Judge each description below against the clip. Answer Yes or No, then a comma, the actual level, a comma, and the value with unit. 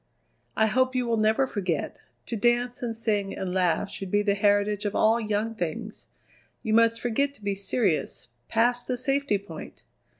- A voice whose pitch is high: Yes, high, 220 Hz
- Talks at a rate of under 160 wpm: No, average, 175 wpm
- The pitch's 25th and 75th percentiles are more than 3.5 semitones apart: No, average, 3.0 semitones